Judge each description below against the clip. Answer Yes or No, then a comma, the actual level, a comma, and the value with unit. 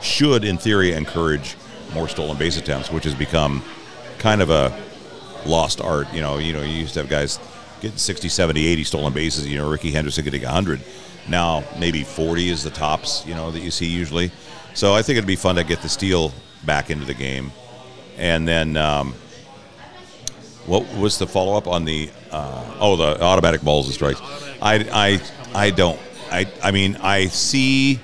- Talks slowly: No, average, 190 wpm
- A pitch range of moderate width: Yes, average, 4.0 semitones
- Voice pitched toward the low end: Yes, very low, 80 Hz